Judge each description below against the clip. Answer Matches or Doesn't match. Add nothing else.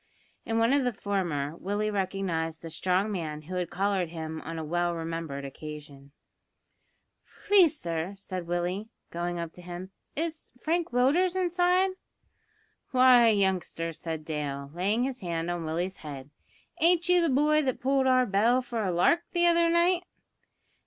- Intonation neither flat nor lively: Doesn't match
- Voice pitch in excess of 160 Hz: Matches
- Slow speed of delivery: Doesn't match